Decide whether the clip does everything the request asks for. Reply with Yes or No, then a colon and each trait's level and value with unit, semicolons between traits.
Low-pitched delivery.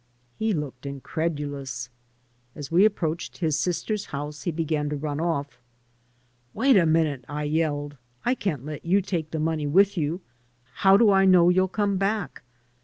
No: medium, 160 Hz